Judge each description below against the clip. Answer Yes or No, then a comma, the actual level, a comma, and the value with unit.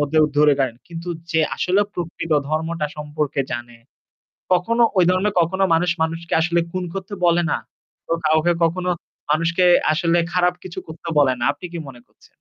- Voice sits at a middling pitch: Yes, medium, 165 Hz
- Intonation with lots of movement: No, average, 2.7 semitones